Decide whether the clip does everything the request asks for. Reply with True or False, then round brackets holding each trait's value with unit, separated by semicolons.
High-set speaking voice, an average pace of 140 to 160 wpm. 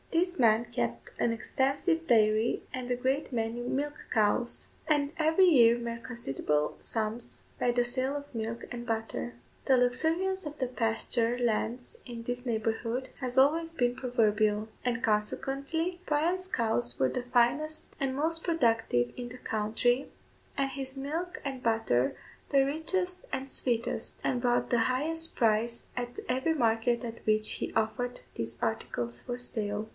True (245 Hz; 150 wpm)